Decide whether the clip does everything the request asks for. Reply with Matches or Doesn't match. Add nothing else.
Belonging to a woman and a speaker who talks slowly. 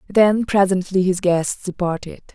Matches